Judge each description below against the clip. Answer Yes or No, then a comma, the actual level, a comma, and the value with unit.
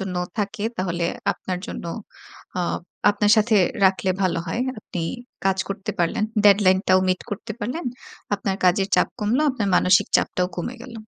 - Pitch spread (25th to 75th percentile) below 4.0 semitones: Yes, narrow, 2.4 semitones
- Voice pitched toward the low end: No, high, 195 Hz